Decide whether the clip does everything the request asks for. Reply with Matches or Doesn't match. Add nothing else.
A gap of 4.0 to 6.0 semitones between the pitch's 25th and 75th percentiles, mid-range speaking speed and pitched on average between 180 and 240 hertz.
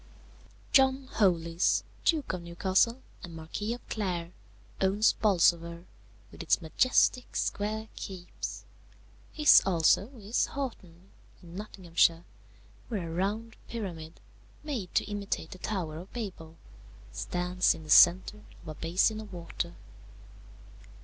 Doesn't match